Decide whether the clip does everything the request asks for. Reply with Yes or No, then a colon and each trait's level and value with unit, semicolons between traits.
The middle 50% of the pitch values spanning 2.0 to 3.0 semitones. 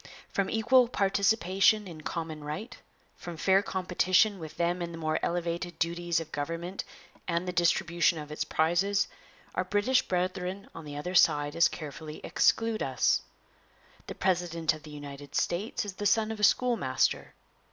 No: average, 3.6 semitones